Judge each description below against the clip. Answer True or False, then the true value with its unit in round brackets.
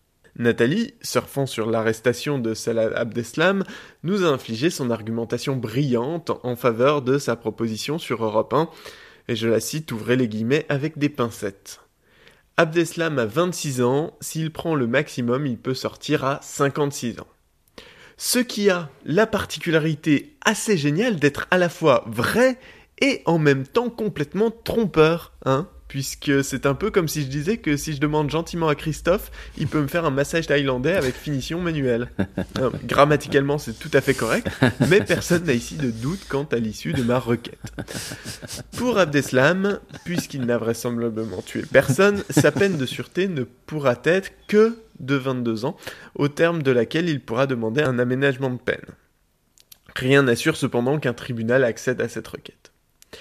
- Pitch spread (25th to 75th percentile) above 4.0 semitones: True (4.9 semitones)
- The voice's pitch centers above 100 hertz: True (140 Hz)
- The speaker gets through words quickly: False (165 wpm)